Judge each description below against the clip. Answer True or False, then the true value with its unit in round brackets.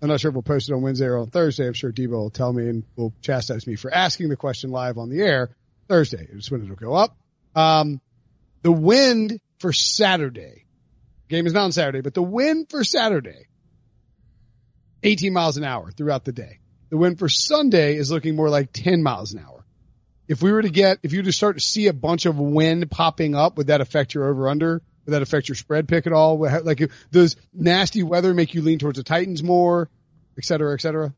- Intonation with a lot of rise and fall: False (4.9 semitones)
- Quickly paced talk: True (225 wpm)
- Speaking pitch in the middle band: True (155 Hz)